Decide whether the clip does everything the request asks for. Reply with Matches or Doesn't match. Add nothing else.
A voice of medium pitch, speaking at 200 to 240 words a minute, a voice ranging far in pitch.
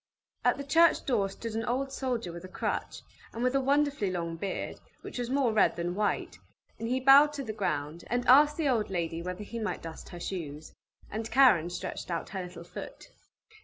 Doesn't match